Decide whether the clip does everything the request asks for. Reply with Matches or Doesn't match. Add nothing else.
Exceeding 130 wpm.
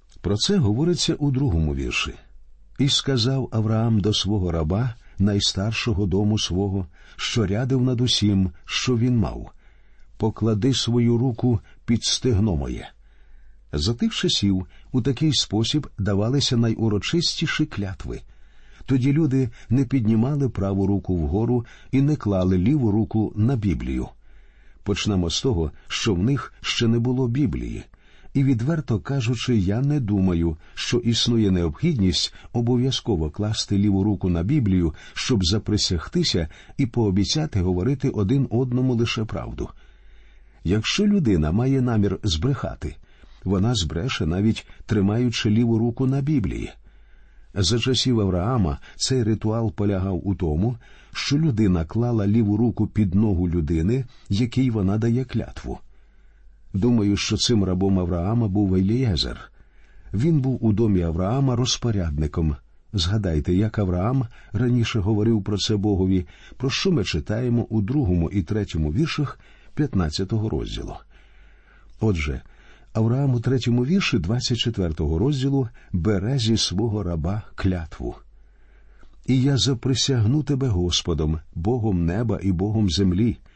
Doesn't match